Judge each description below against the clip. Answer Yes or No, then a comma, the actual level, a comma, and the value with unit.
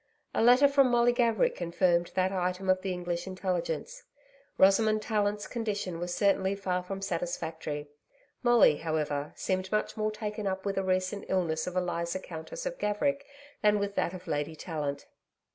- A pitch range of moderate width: Yes, average, 3.3 semitones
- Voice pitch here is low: No, high, 190 Hz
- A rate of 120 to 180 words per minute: Yes, average, 160 wpm